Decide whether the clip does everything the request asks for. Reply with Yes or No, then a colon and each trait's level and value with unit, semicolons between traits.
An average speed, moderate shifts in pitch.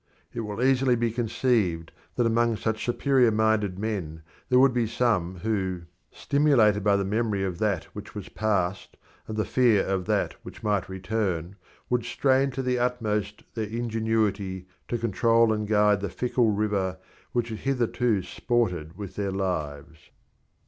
Yes: average, 160 wpm; average, 3.5 semitones